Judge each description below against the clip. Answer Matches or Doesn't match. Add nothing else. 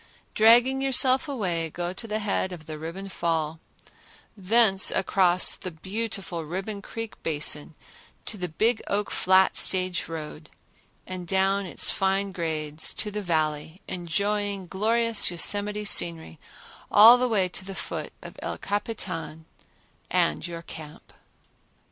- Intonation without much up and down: Doesn't match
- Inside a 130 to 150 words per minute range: Matches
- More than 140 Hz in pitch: Matches